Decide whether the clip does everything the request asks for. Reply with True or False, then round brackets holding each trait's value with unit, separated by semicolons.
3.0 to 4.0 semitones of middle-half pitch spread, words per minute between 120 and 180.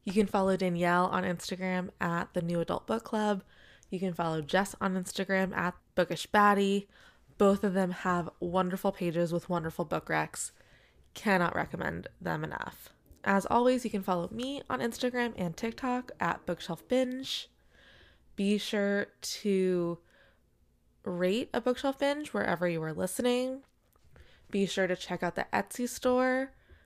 False (4.4 semitones; 150 wpm)